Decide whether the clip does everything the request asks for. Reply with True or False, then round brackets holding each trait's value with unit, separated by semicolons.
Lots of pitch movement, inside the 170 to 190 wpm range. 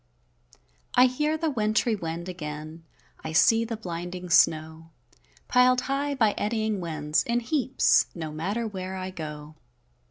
False (6.5 semitones; 135 wpm)